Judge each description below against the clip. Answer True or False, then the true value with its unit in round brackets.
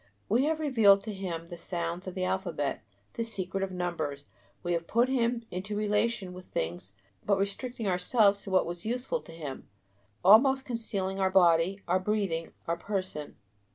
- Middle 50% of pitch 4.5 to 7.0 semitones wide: False (4.1 semitones)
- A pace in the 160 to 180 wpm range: True (170 wpm)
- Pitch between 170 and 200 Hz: True (190 Hz)